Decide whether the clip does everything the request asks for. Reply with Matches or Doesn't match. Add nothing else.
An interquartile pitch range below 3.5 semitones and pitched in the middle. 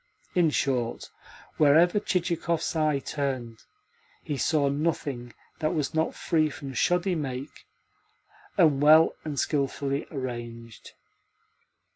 Matches